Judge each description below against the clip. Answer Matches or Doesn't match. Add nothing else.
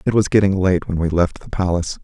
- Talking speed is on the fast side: Matches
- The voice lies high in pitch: Doesn't match